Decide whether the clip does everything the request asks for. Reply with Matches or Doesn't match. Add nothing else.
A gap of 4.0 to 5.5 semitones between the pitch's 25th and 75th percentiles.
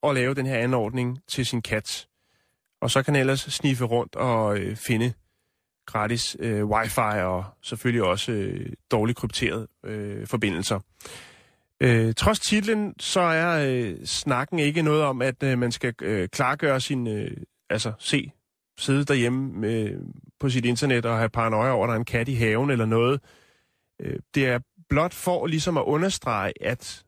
Doesn't match